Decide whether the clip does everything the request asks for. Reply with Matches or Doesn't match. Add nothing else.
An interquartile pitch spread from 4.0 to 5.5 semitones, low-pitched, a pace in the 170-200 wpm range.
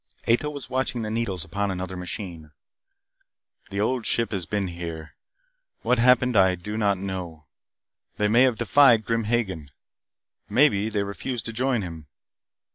Doesn't match